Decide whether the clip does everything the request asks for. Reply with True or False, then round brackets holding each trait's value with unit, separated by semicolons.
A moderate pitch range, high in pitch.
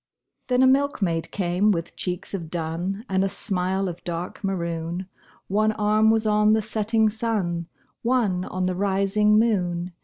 True (3.4 semitones; 195 Hz)